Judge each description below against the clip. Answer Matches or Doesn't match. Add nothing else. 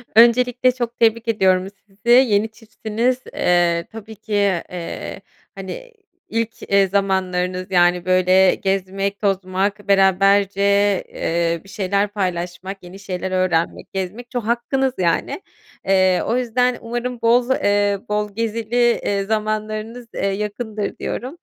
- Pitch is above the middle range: Matches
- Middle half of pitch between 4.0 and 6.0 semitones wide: Doesn't match